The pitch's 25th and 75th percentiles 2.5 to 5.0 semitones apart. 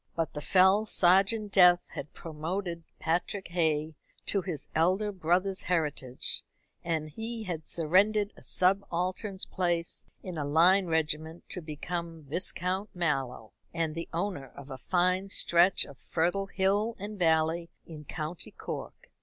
Yes: average, 3.1 semitones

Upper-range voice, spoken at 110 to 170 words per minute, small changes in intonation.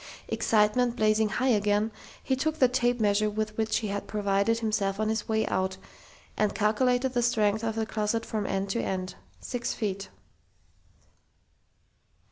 Yes: high, 215 Hz; average, 155 wpm; narrow, 2.2 semitones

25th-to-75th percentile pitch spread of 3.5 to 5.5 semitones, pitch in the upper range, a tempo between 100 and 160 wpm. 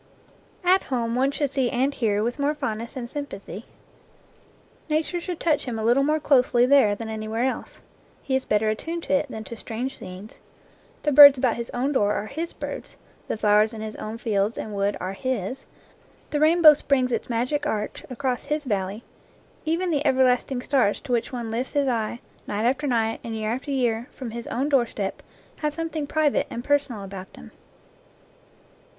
No: average, 4.4 semitones; very high, 250 Hz; average, 190 wpm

